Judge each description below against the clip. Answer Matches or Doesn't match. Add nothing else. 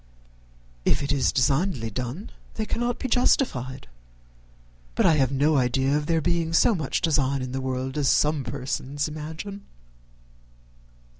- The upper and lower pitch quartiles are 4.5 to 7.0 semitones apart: Doesn't match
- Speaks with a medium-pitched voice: Matches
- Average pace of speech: Matches